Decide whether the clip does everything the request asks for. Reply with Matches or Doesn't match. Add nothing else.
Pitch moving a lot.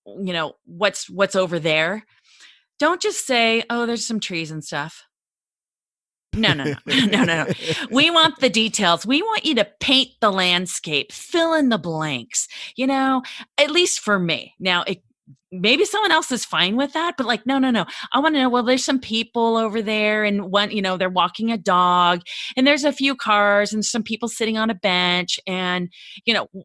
Matches